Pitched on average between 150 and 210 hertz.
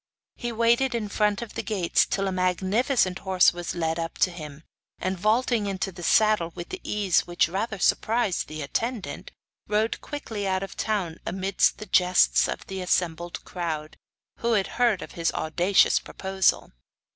Yes: high, 190 Hz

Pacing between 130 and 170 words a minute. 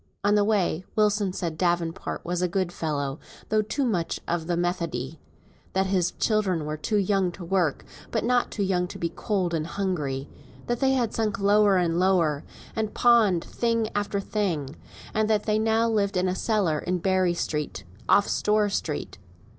No: average, 180 wpm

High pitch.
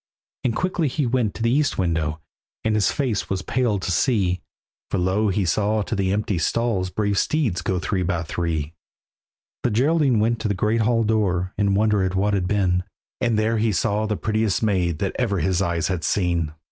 No: low, 100 Hz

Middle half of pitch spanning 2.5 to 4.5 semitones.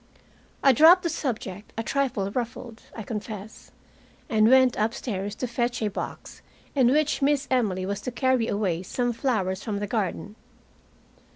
Yes: average, 4.0 semitones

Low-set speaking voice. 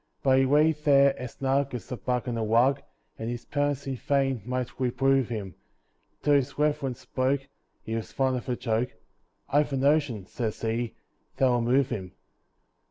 Yes: low, 130 Hz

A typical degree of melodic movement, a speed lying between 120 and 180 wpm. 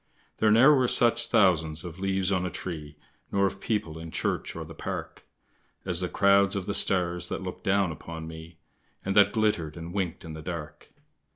No: average, 3.3 semitones; average, 195 wpm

